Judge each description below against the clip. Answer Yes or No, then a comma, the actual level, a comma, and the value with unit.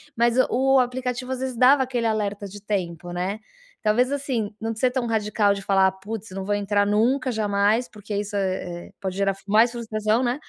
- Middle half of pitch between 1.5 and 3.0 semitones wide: No, average, 3.5 semitones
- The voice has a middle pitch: No, high, 215 Hz